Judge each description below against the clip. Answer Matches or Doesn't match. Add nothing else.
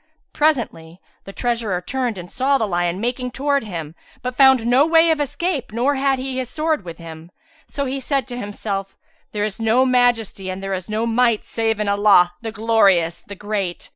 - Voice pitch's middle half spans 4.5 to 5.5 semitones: Matches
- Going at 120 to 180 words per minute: Doesn't match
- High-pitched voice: Matches